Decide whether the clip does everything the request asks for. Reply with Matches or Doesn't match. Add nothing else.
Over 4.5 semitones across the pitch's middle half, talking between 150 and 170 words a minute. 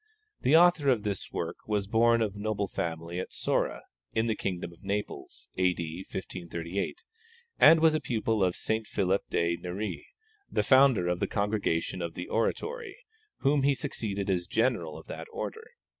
Matches